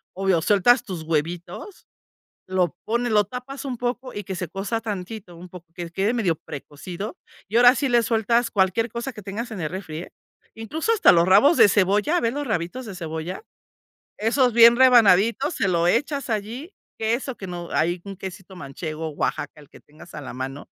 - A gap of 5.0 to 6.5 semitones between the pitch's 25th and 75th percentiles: Yes, average, 5.3 semitones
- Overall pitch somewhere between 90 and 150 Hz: No, high, 200 Hz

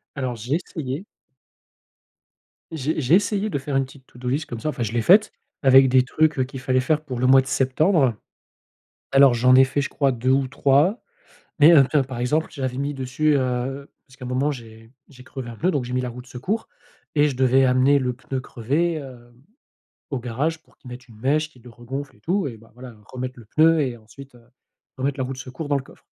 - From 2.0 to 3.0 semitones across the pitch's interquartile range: Yes, average, 2.7 semitones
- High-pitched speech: No, low, 130 Hz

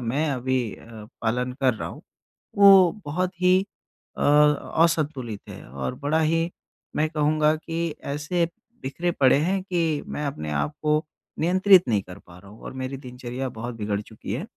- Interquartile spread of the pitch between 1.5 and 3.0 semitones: No, average, 5.1 semitones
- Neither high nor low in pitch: Yes, medium, 145 Hz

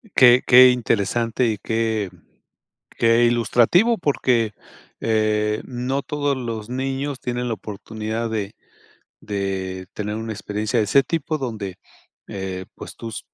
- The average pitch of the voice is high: No, low, 115 Hz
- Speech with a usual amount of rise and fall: Yes, average, 3.0 semitones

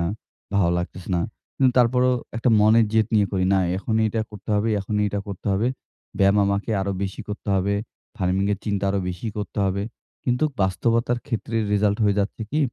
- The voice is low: Yes, low, 105 Hz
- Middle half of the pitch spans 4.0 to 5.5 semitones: No, narrow, 2.6 semitones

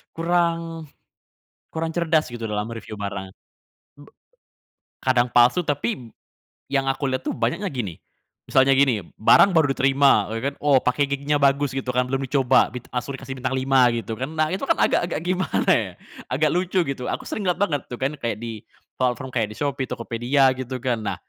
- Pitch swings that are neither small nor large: Yes, average, 3.4 semitones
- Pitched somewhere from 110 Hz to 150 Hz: Yes, low, 135 Hz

